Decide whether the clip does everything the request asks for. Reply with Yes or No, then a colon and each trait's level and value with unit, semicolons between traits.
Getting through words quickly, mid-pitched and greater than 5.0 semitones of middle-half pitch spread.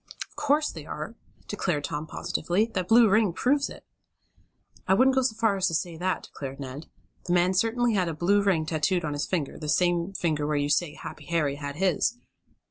Yes: fast, 210 wpm; medium, 175 Hz; wide, 5.4 semitones